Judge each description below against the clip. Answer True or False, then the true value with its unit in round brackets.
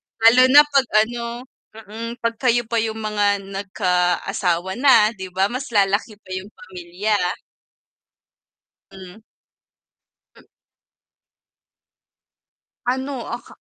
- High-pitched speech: True (215 Hz)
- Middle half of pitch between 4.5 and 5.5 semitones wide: False (3.7 semitones)